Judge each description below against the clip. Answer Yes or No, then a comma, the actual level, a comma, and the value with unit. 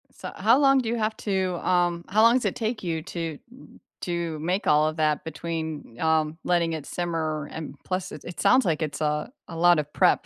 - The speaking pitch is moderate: Yes, medium, 170 Hz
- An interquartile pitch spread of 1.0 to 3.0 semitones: No, average, 3.4 semitones